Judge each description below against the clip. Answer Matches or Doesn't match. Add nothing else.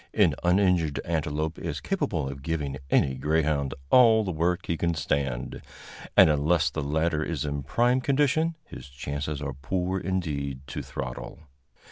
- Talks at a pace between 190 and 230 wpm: Doesn't match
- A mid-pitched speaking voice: Doesn't match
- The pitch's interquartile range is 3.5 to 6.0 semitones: Matches